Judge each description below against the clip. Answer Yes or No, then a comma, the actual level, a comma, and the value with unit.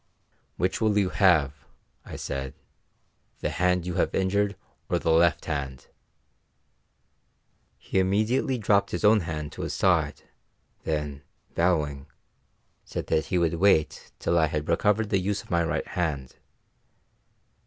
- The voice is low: Yes, very low, 85 Hz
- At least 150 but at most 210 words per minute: No, slow, 135 wpm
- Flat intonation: No, average, 4.4 semitones